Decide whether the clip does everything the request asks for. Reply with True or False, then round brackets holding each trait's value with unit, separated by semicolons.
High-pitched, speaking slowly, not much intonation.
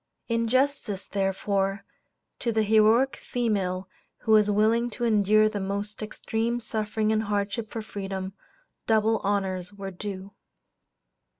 True (210 Hz; 125 wpm; 2.1 semitones)